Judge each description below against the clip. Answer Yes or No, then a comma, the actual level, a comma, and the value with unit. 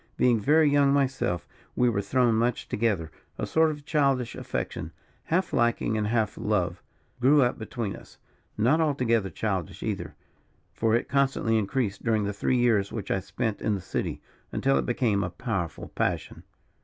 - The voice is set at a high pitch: No, low, 115 Hz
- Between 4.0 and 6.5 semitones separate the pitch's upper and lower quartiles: Yes, average, 4.5 semitones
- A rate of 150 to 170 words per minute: Yes, average, 165 wpm